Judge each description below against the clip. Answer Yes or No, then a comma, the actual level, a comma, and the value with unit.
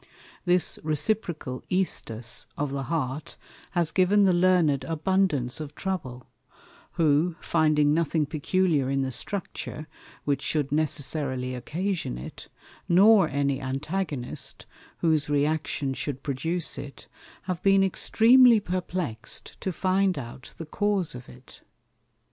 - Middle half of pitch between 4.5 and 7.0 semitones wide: Yes, average, 5.1 semitones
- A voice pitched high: No, medium, 155 Hz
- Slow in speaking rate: Yes, slow, 120 wpm